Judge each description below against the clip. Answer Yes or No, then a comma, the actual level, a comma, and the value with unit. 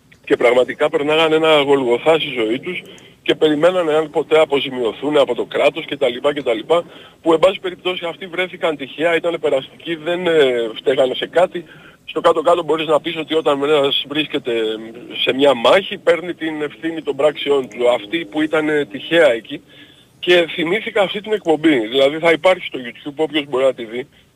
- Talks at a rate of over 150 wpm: Yes, fast, 170 wpm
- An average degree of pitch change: Yes, average, 3.1 semitones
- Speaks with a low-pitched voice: No, medium, 155 Hz